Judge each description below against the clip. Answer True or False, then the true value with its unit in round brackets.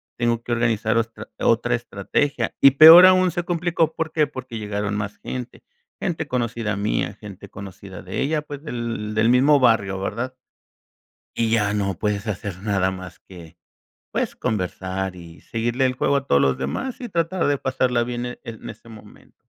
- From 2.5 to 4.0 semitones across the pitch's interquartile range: False (5.2 semitones)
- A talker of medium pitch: False (115 Hz)